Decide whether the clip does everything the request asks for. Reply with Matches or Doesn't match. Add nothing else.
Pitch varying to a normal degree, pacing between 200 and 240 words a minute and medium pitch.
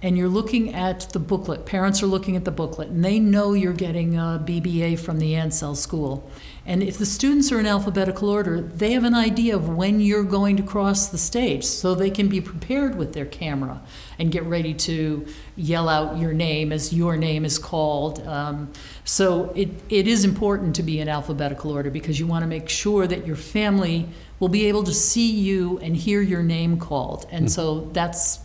Matches